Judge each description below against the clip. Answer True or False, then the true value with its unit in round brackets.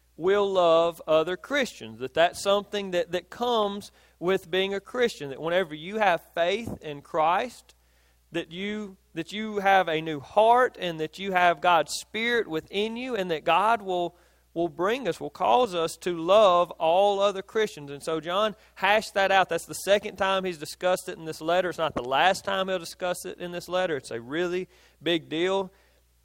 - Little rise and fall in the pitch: False (3.6 semitones)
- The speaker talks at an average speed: True (190 wpm)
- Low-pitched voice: False (180 Hz)